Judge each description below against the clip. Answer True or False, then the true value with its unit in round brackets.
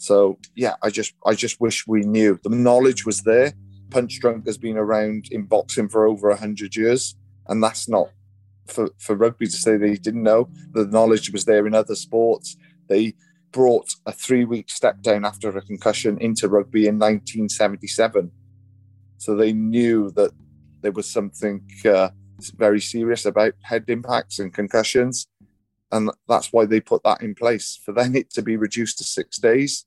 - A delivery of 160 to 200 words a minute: True (175 wpm)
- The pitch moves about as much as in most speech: False (2.1 semitones)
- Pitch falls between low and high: False (110 Hz)